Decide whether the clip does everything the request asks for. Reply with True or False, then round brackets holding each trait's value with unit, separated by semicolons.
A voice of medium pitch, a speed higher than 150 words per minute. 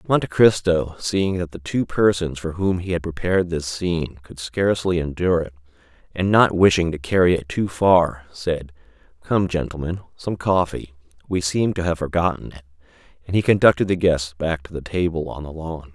False (85 Hz; 180 wpm)